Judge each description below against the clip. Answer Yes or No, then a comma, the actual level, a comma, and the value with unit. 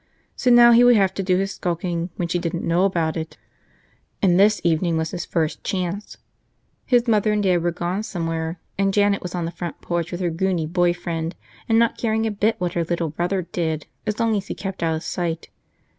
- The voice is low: No, medium, 180 Hz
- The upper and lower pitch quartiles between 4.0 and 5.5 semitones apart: No, average, 3.2 semitones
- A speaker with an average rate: No, fast, 220 wpm